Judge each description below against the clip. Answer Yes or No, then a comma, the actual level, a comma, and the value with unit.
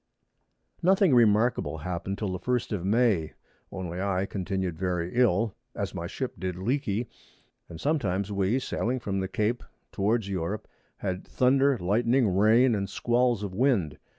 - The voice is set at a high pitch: No, low, 105 Hz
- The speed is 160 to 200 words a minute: No, average, 150 wpm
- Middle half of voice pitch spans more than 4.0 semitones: Yes, average, 4.6 semitones